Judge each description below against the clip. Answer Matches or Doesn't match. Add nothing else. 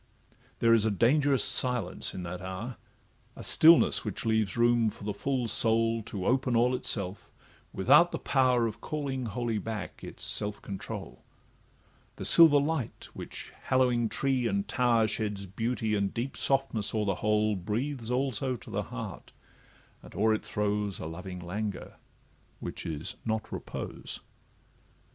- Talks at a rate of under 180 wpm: Matches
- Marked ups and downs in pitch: Doesn't match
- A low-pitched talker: Matches